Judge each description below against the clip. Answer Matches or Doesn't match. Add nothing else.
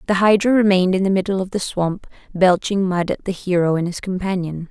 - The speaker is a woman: Matches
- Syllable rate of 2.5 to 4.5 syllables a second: Doesn't match